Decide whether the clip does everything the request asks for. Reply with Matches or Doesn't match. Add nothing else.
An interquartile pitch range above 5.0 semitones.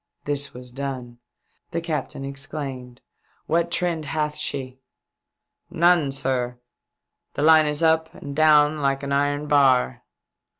Doesn't match